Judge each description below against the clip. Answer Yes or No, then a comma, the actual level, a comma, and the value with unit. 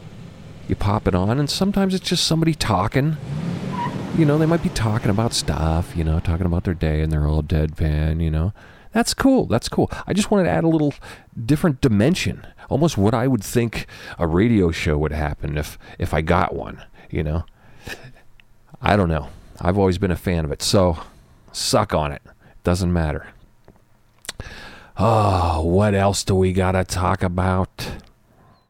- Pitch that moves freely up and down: Yes, wide, 7.4 semitones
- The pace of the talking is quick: No, average, 180 wpm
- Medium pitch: No, low, 100 Hz